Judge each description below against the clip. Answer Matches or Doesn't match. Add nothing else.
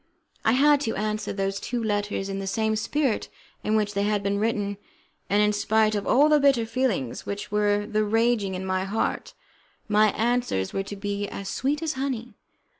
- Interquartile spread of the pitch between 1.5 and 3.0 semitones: Matches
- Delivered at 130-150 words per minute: Doesn't match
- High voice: Matches